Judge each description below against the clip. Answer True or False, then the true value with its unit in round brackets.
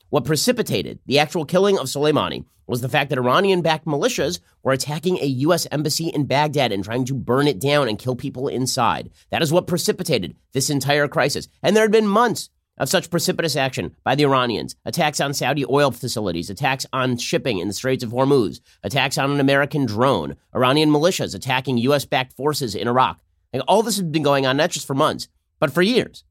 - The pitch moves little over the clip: False (3.5 semitones)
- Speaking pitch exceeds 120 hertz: True (140 Hz)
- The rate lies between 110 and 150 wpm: False (205 wpm)